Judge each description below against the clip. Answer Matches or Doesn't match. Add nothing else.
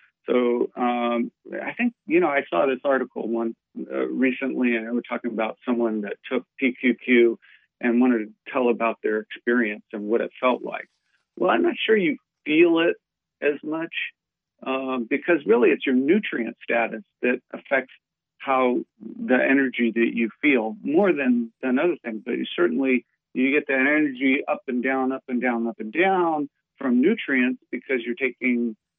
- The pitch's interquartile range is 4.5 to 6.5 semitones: Doesn't match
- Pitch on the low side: Matches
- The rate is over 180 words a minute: Doesn't match